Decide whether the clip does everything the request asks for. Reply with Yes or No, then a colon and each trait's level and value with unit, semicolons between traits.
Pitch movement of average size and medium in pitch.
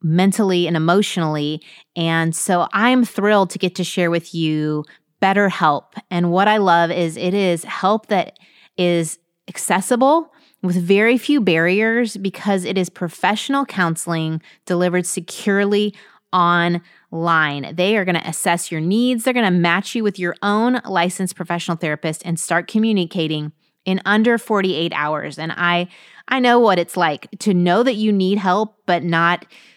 Yes: average, 3.5 semitones; medium, 180 Hz